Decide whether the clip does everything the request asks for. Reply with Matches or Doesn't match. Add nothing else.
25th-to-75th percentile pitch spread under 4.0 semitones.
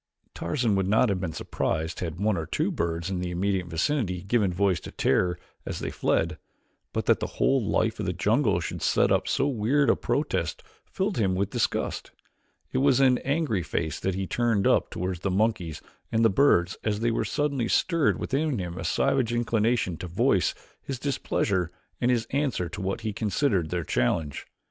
Doesn't match